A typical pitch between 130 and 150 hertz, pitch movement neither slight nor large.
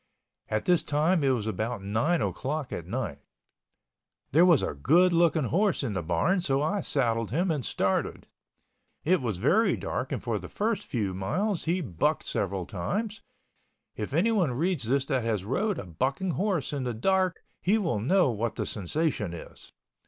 No: medium, 140 Hz; wide, 8.5 semitones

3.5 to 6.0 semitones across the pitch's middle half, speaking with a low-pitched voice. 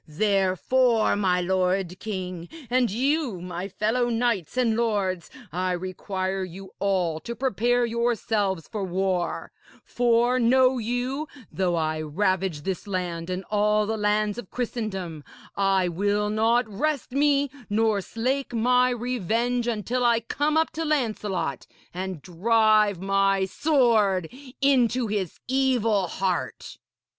No: average, 4.4 semitones; high, 210 Hz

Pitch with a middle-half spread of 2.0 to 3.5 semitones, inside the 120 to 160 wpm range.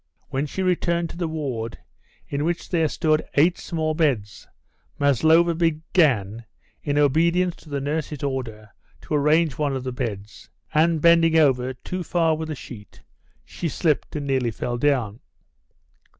No: average, 4.1 semitones; average, 150 wpm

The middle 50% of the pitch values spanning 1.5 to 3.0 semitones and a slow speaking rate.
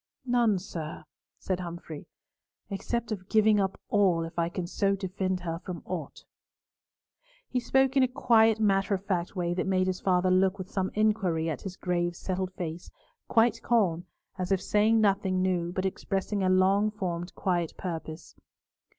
No: average, 2.7 semitones; average, 165 wpm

